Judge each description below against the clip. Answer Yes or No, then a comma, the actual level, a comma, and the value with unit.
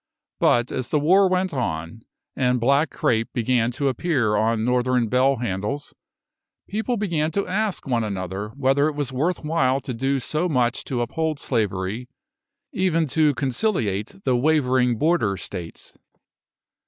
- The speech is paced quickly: No, average, 145 wpm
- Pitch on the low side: Yes, low, 130 Hz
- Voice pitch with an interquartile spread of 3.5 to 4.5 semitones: No, average, 5.1 semitones